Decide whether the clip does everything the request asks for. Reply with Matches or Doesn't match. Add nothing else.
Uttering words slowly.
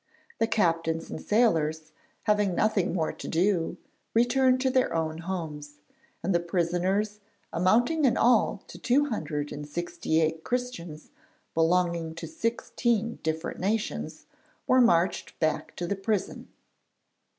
Matches